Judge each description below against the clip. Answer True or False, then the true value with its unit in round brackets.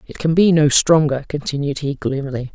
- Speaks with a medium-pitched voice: True (145 Hz)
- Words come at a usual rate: True (190 wpm)